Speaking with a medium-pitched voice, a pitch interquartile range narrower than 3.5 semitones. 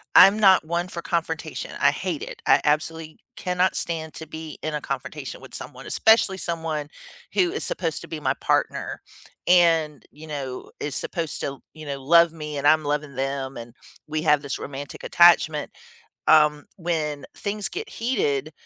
Yes: medium, 155 Hz; average, 2.7 semitones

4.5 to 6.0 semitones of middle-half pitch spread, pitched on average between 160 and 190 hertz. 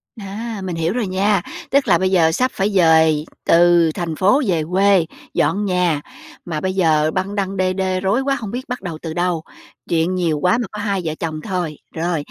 No: average, 3.3 semitones; medium, 185 Hz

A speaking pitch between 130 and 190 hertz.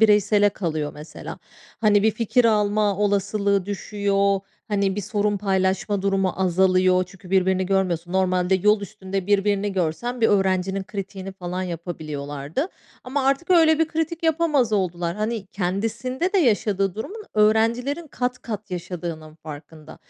No: high, 200 Hz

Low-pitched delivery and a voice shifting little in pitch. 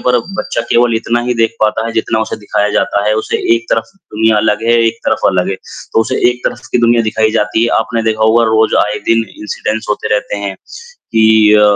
Yes: low, 110 Hz; narrow, 1.4 semitones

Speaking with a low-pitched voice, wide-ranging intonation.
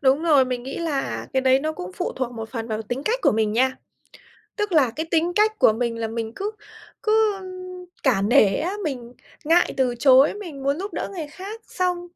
No: very high, 270 Hz; wide, 6.5 semitones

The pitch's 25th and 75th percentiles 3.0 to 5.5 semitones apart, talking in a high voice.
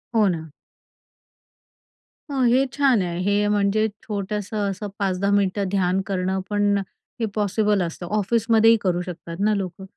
No: narrow, 2.4 semitones; high, 200 Hz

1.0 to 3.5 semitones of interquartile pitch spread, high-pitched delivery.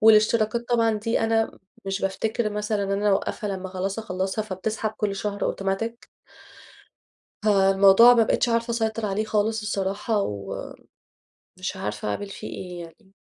Yes: narrow, 2.4 semitones; high, 210 Hz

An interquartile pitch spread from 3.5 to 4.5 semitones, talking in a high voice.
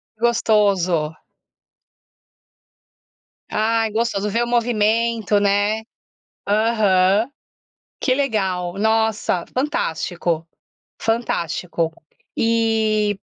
No: average, 3.1 semitones; high, 215 Hz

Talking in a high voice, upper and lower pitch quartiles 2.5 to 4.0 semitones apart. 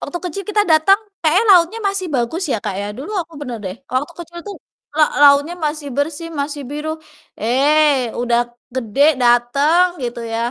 No: very high, 295 Hz; average, 5.3 semitones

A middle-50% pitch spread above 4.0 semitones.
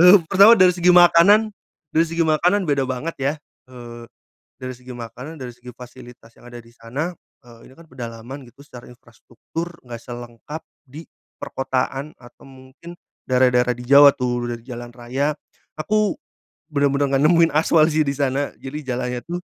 Yes: average, 4.6 semitones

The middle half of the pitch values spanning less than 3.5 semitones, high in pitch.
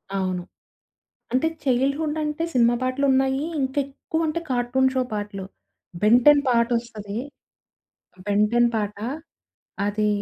No: average, 4.3 semitones; high, 245 Hz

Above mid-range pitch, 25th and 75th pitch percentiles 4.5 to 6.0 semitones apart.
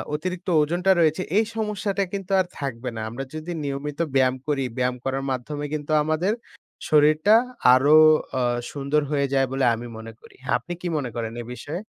No: medium, 145 Hz; average, 4.8 semitones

